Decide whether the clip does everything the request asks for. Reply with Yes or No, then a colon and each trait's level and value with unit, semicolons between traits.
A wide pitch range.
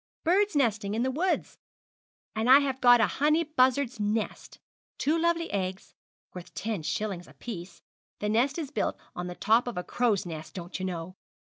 Yes: wide, 6.9 semitones